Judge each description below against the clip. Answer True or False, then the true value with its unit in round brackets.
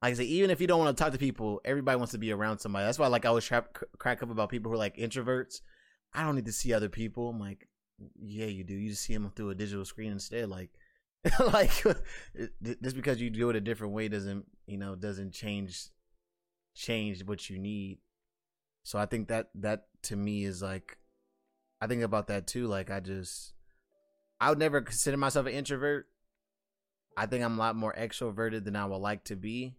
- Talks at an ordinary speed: False (220 wpm)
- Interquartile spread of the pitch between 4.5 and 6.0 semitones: False (3.4 semitones)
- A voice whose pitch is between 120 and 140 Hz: False (110 Hz)